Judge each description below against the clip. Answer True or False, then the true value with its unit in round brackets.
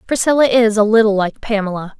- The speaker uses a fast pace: False (180 wpm)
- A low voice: False (220 Hz)